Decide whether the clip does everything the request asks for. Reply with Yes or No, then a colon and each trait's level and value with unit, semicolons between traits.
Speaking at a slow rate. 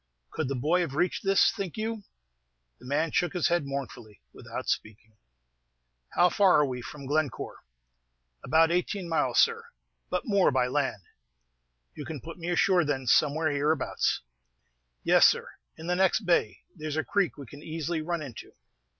No: average, 165 wpm